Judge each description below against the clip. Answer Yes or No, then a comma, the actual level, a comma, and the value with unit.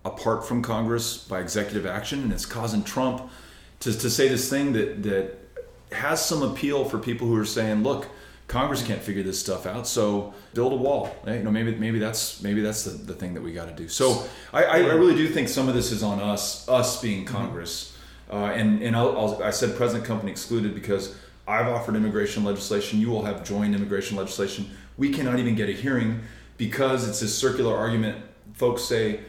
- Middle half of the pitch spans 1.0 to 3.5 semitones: Yes, average, 2.9 semitones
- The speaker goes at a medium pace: No, fast, 210 wpm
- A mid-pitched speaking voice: No, low, 110 Hz